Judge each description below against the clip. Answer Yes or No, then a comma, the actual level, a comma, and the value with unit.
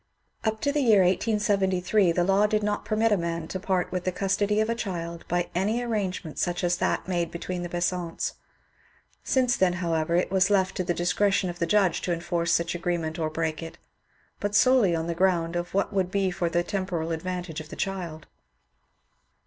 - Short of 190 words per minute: No, average, 200 wpm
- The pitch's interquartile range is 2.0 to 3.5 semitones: Yes, average, 2.9 semitones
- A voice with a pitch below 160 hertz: No, medium, 180 Hz